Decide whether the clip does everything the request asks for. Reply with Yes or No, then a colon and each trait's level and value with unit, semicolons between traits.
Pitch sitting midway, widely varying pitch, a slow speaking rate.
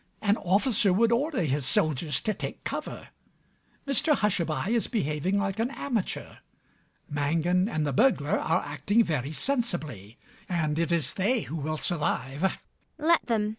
No: medium, 180 Hz; wide, 7.0 semitones; average, 150 wpm